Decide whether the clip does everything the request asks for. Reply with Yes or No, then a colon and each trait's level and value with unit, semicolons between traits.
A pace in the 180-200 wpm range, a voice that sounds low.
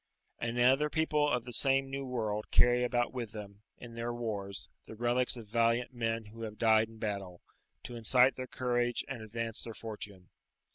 Yes: average, 185 wpm; low, 115 Hz